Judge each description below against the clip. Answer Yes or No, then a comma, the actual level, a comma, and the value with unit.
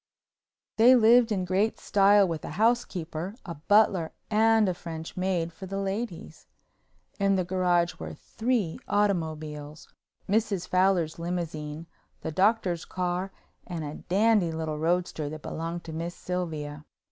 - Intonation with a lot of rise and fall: No, average, 3.8 semitones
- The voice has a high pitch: No, medium, 180 Hz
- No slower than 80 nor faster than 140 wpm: Yes, slow, 135 wpm